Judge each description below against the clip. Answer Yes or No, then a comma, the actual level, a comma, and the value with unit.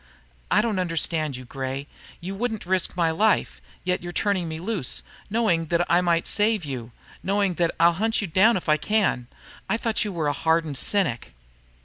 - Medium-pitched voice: Yes, medium, 175 Hz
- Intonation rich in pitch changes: No, average, 4.4 semitones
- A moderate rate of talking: Yes, average, 190 wpm